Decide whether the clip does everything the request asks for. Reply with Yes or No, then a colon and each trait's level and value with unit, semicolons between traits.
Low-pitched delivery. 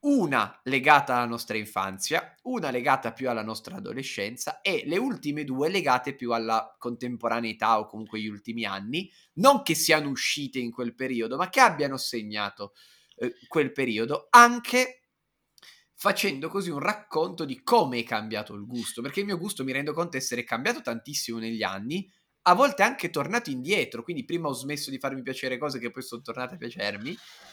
Yes: low, 130 Hz